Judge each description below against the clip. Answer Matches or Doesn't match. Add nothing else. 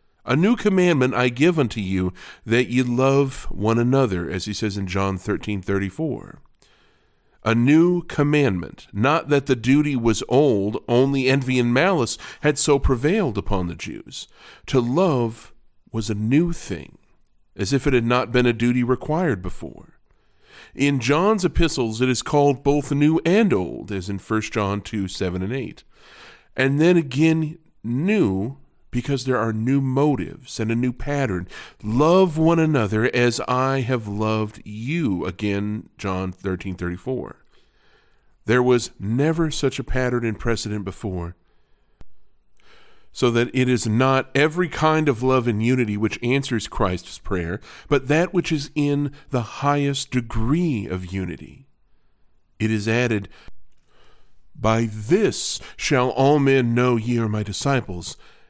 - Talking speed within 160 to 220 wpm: Doesn't match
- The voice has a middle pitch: Doesn't match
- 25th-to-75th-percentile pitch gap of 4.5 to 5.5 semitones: Matches